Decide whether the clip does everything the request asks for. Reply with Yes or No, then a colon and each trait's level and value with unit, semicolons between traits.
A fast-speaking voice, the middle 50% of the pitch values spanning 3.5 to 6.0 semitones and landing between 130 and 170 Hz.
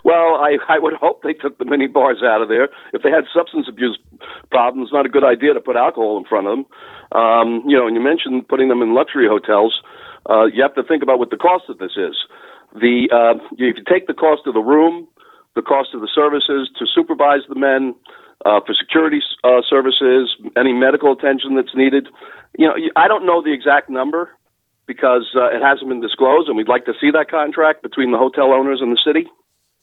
Yes: fast, 225 wpm; average, 3.9 semitones; medium, 140 Hz